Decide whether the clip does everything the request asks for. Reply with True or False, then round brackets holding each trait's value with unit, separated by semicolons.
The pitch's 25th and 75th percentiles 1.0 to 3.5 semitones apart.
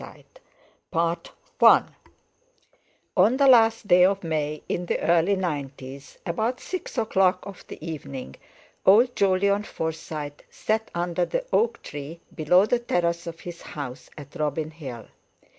False (4.7 semitones)